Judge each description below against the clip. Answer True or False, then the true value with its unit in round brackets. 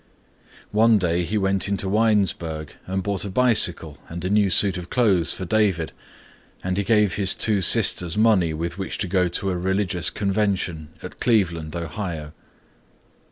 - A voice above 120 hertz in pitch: False (95 Hz)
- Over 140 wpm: True (160 wpm)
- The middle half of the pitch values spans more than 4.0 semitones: False (3.3 semitones)